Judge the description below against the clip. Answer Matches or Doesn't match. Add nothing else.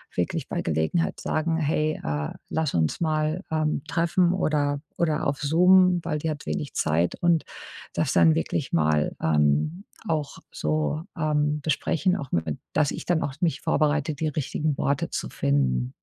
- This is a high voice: Doesn't match